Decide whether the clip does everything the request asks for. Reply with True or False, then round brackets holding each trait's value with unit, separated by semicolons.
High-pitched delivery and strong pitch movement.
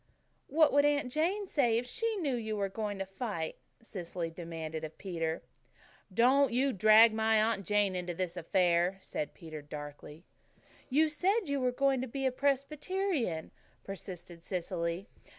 True (215 Hz; 7.9 semitones)